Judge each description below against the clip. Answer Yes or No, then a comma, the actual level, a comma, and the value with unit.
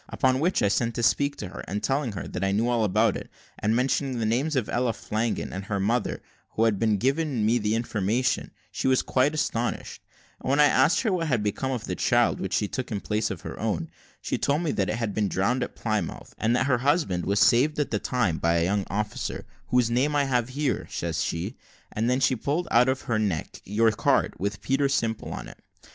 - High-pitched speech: No, low, 120 Hz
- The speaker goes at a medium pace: No, fast, 235 wpm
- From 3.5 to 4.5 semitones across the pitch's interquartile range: Yes, average, 4.1 semitones